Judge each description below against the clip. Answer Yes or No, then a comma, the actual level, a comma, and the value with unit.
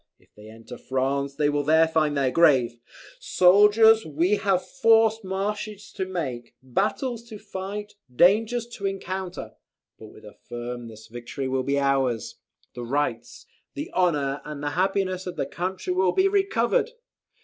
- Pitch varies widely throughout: Yes, wide, 7.3 semitones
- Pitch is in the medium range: Yes, medium, 175 Hz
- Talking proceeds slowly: No, average, 150 wpm